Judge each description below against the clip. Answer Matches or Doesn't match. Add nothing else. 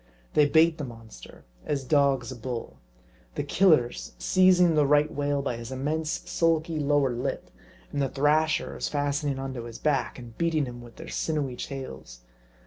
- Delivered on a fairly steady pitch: Doesn't match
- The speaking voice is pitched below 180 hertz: Matches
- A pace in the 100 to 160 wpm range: Doesn't match